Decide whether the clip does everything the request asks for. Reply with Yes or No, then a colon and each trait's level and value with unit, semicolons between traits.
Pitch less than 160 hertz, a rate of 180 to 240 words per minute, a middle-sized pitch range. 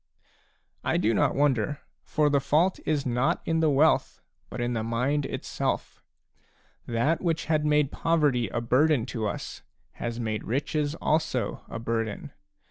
No: medium, 140 Hz; average, 150 wpm; average, 4.6 semitones